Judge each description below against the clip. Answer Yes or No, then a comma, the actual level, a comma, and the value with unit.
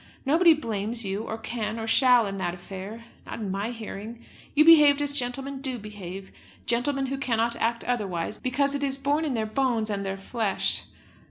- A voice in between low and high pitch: No, high, 235 Hz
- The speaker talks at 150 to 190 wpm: Yes, average, 185 wpm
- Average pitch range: Yes, average, 4.6 semitones